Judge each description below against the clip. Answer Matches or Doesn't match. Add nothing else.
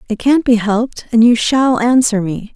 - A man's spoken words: Doesn't match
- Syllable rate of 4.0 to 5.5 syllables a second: Matches